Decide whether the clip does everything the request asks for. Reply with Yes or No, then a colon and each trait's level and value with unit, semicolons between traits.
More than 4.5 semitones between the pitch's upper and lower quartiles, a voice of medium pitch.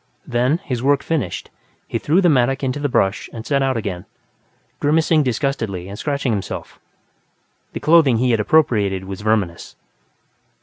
No: wide, 5.5 semitones; low, 125 Hz